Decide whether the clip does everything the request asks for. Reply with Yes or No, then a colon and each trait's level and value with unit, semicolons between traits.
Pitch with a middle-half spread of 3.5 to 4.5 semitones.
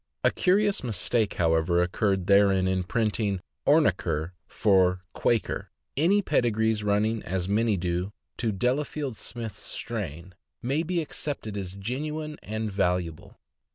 No: average, 5.0 semitones